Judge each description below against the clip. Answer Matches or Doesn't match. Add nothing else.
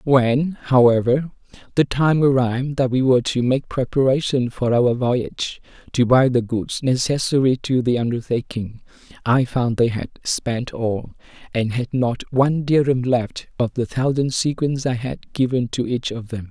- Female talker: Doesn't match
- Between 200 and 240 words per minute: Doesn't match